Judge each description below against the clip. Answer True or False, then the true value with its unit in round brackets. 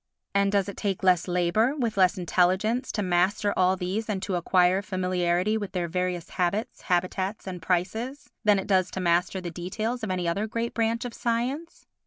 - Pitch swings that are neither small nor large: True (3.2 semitones)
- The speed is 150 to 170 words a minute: False (190 wpm)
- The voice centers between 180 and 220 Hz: True (190 Hz)